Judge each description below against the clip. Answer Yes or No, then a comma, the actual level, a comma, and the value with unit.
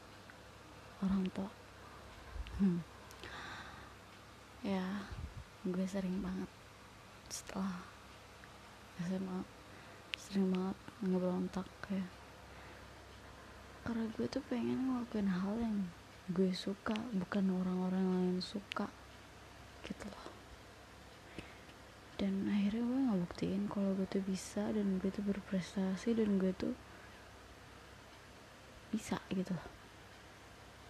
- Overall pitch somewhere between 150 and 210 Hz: Yes, medium, 185 Hz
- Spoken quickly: No, average, 90 wpm